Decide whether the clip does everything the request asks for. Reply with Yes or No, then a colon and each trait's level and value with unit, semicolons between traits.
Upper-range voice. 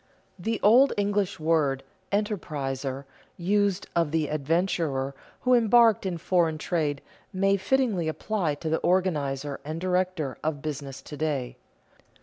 No: medium, 165 Hz